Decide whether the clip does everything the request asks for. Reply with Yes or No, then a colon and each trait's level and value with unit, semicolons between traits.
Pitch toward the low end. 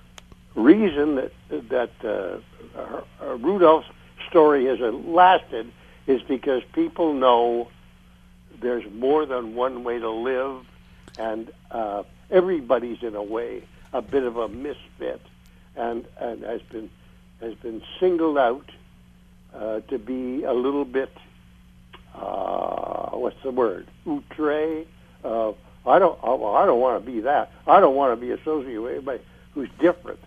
Yes: low, 120 Hz